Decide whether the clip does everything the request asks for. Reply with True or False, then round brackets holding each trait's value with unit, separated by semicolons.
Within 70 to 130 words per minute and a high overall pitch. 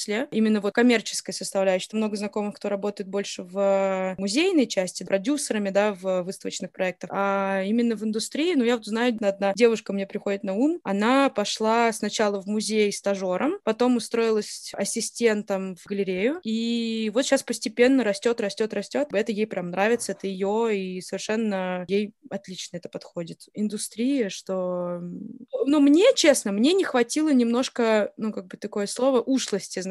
False (155 wpm; 210 Hz)